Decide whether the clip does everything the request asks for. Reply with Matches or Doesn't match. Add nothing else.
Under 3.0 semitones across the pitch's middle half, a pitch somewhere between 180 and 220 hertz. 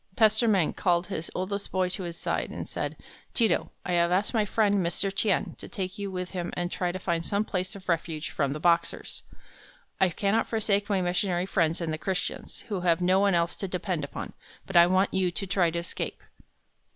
Matches